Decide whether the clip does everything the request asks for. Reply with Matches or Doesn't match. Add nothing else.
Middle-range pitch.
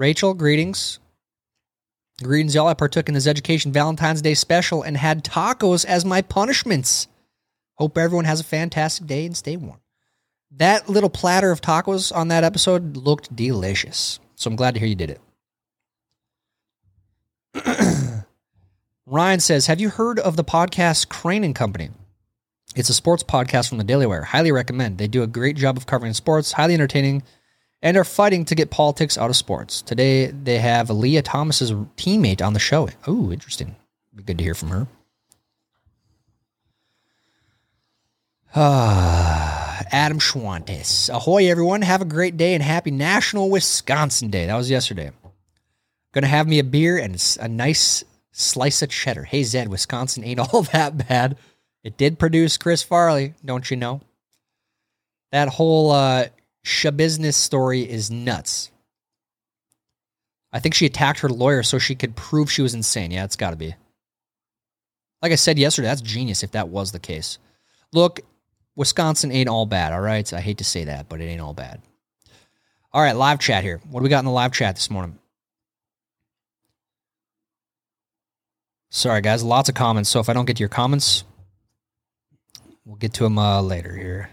Doesn't match